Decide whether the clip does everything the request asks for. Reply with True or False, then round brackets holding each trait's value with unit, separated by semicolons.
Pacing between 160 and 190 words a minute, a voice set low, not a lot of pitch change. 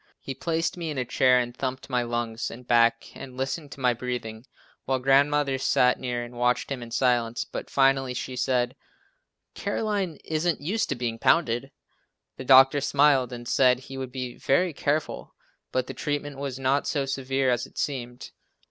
True (180 wpm; 130 Hz; 2.3 semitones)